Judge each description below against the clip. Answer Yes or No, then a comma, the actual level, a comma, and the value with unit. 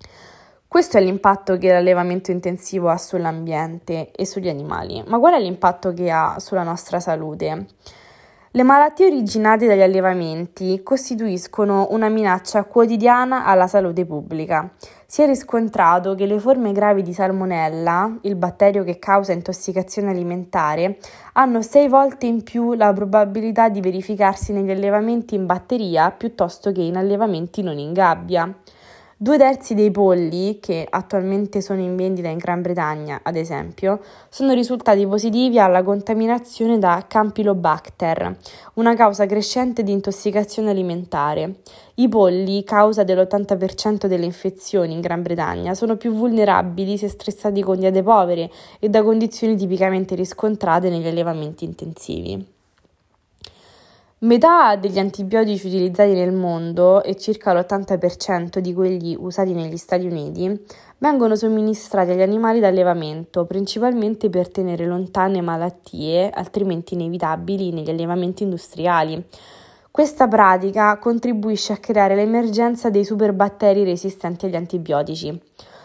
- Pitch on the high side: Yes, high, 195 Hz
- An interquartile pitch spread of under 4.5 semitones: Yes, average, 3.3 semitones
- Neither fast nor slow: Yes, average, 125 wpm